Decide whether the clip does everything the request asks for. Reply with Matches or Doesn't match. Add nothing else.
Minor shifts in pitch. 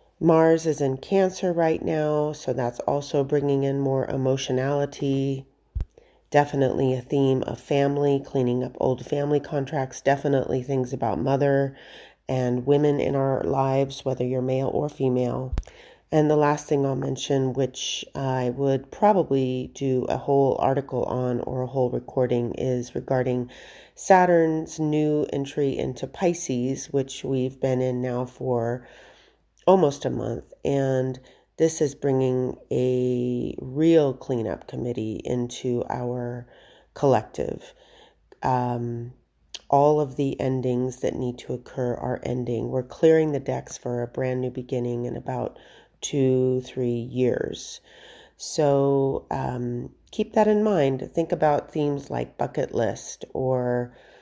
Matches